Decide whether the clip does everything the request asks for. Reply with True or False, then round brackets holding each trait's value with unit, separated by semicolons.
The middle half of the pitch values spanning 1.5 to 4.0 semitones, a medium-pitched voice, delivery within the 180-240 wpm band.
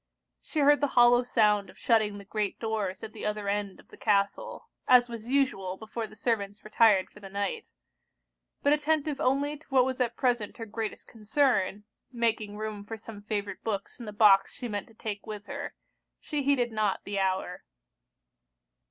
False (3.3 semitones; 220 Hz; 185 wpm)